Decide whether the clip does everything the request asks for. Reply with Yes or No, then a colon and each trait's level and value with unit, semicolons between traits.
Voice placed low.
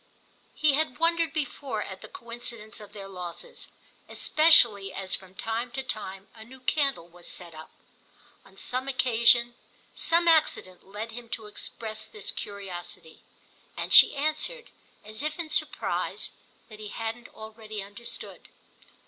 No: high, 225 Hz